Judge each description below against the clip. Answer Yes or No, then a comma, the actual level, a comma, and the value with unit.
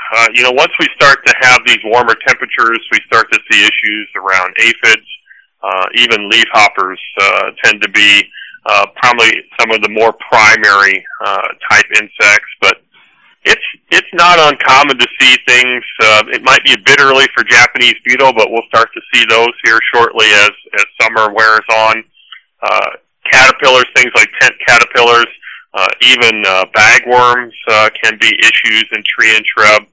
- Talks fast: No, average, 170 wpm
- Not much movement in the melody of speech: Yes, narrow, 2.1 semitones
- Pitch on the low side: Yes, low, 115 Hz